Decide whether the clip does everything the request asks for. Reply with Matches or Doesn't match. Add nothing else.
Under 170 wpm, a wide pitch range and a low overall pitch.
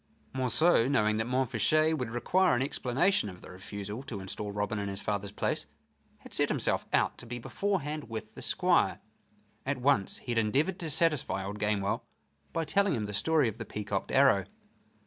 Doesn't match